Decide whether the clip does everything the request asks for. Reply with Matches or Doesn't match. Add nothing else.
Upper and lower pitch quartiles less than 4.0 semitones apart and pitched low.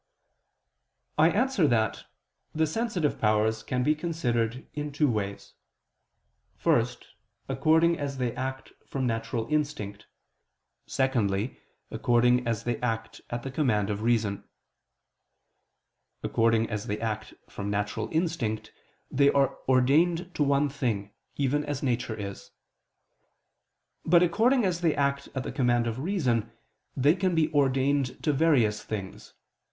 Doesn't match